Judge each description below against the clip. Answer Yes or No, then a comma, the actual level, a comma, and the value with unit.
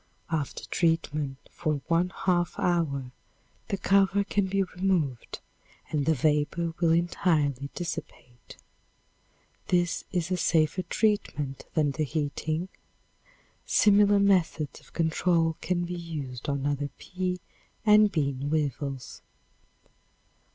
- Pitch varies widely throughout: No, average, 3.9 semitones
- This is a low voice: No, medium, 165 Hz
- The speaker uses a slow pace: Yes, slow, 110 wpm